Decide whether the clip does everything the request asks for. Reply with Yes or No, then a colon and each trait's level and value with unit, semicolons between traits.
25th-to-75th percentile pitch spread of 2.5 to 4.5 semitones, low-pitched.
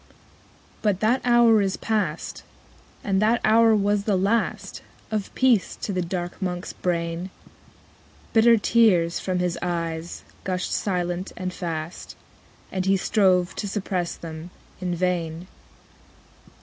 No: average, 3.2 semitones; medium, 185 Hz